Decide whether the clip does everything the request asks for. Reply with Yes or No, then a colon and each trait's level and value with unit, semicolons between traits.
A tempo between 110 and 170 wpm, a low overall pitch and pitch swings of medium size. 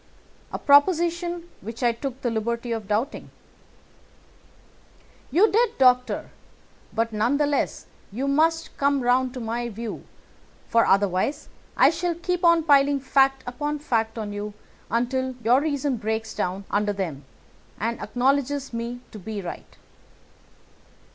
No: slow, 135 wpm; very high, 250 Hz; average, 4.4 semitones